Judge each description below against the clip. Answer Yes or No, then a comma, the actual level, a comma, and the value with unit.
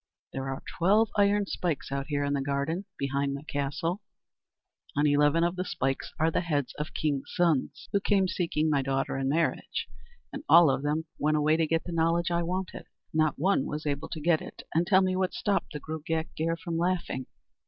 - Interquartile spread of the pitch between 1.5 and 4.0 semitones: Yes, average, 3.4 semitones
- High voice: No, medium, 160 Hz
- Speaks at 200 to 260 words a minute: Yes, fast, 205 wpm